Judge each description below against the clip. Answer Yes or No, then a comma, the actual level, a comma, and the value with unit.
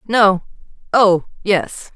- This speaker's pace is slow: Yes, slow, 90 wpm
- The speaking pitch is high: Yes, high, 195 Hz